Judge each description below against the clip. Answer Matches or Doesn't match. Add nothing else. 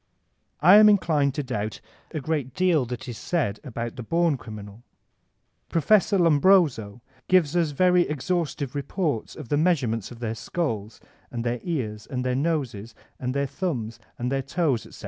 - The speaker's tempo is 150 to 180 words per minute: Matches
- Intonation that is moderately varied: Doesn't match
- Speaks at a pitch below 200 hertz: Matches